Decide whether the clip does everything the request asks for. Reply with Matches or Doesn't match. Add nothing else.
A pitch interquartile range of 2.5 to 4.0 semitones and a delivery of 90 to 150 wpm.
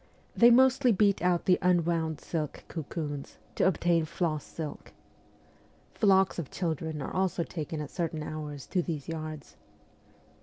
Matches